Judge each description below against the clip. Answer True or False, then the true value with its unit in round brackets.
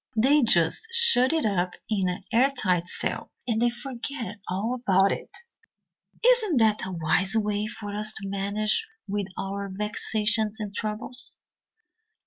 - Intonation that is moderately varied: True (3.5 semitones)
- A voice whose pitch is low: False (215 Hz)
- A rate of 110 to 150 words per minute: True (140 wpm)